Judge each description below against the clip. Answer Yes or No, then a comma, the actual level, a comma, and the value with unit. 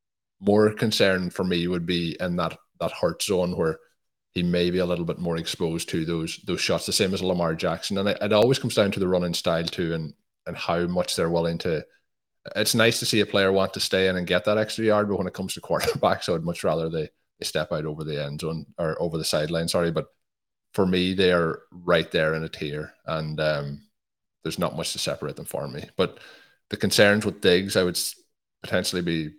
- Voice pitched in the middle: No, very low, 90 Hz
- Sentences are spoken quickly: Yes, fast, 235 wpm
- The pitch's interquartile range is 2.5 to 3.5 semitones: Yes, average, 2.9 semitones